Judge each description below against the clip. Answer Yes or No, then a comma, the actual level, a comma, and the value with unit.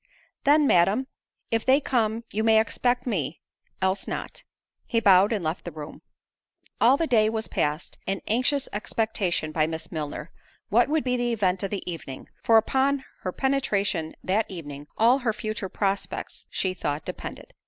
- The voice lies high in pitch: Yes, high, 215 Hz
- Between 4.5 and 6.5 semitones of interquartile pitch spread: Yes, wide, 5.4 semitones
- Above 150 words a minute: Yes, average, 165 wpm